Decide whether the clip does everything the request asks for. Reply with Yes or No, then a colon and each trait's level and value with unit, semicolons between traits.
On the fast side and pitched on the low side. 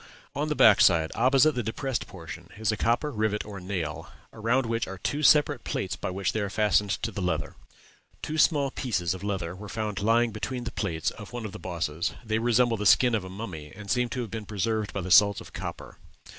Yes: fast, 225 wpm; low, 105 Hz